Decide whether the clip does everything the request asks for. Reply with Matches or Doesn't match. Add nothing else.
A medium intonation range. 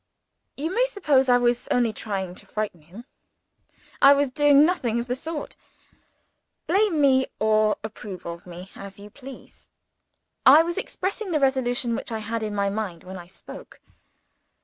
Doesn't match